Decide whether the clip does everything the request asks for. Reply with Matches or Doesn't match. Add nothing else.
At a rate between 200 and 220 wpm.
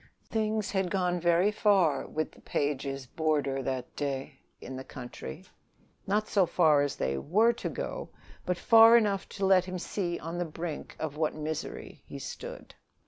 Doesn't match